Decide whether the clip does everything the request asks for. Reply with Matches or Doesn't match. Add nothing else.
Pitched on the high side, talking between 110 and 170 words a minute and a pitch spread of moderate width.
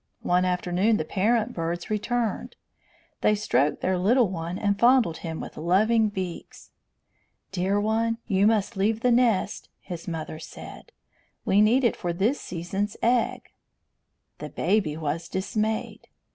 Matches